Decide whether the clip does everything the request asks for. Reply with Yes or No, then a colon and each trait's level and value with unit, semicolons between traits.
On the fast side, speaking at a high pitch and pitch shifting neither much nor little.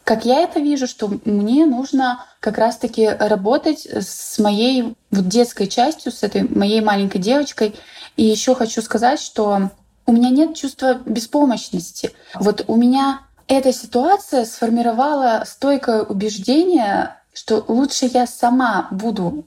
No: average, 130 wpm; high, 240 Hz; average, 3.7 semitones